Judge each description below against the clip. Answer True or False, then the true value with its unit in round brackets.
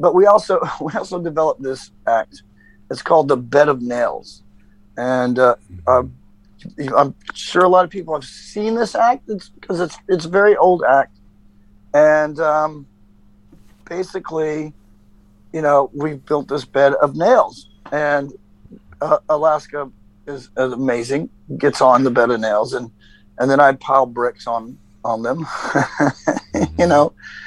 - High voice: False (135 Hz)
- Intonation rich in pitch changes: True (7.2 semitones)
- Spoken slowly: False (150 wpm)